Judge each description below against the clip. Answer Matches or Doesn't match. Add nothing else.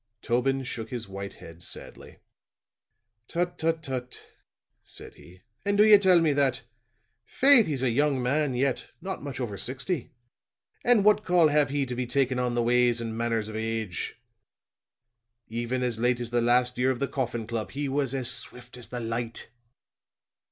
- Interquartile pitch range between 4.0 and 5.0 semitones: Doesn't match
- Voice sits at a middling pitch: Doesn't match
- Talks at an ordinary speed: Matches